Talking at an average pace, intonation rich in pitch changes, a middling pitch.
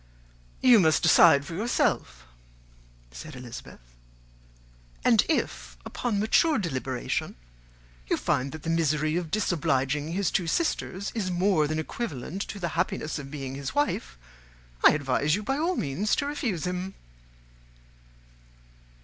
No: slow, 130 wpm; wide, 6.1 semitones; medium, 165 Hz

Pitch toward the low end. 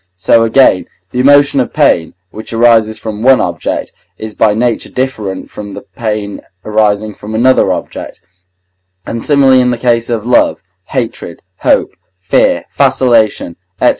Yes: low, 115 Hz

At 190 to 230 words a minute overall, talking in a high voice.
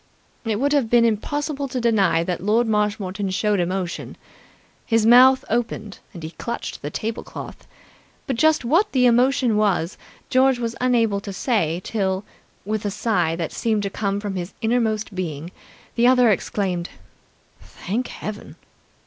No: average, 150 wpm; high, 215 Hz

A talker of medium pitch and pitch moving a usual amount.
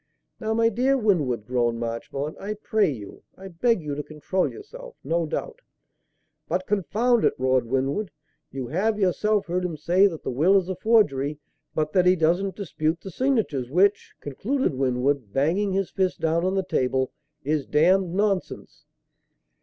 No: medium, 180 Hz; wide, 6.2 semitones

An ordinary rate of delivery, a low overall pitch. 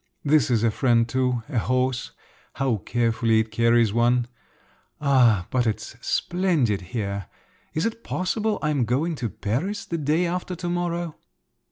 Yes: average, 150 wpm; low, 125 Hz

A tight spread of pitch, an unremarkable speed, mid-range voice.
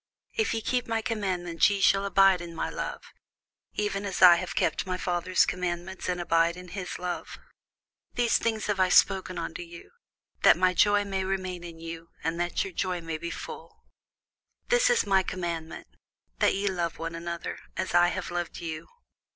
Yes: narrow, 2.3 semitones; average, 185 wpm; medium, 180 Hz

